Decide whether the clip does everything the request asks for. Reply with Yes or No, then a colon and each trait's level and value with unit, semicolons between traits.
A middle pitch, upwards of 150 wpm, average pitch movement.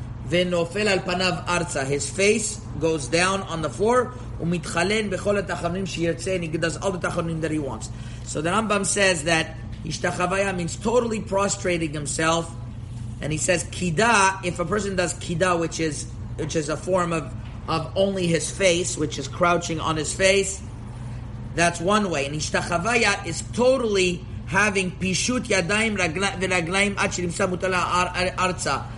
No: medium, 175 Hz; average, 145 wpm; average, 4.1 semitones